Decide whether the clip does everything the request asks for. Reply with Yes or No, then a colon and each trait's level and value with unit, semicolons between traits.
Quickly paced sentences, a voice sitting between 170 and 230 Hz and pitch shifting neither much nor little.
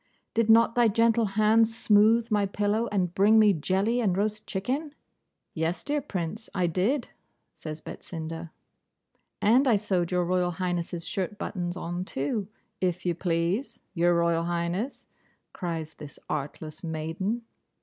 No: average, 140 wpm; high, 190 Hz; average, 4.5 semitones